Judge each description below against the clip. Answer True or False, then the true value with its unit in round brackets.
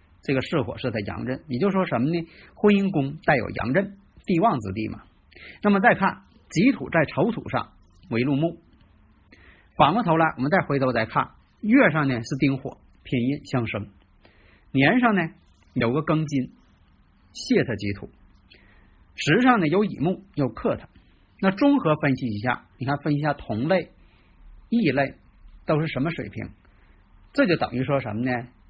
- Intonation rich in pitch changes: True (7.4 semitones)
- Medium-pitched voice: False (130 Hz)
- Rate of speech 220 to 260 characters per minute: True (230 characters per minute)